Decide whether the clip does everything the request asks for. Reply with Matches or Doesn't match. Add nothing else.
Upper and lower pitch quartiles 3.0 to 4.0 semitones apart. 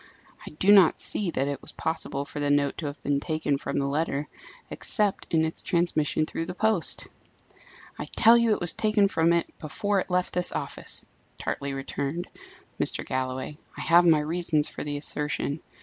Matches